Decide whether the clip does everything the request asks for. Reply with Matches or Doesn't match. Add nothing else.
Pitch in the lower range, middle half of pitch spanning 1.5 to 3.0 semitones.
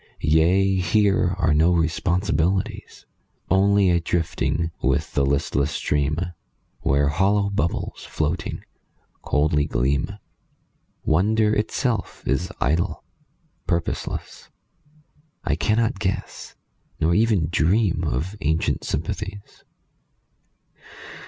Doesn't match